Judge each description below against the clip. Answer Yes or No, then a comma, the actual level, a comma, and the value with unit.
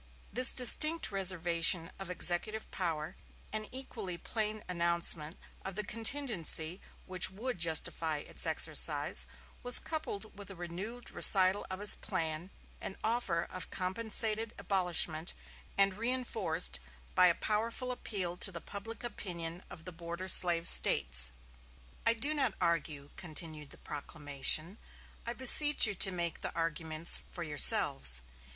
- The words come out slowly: Yes, slow, 130 wpm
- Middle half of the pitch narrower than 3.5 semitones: No, average, 4.7 semitones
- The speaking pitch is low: No, medium, 185 Hz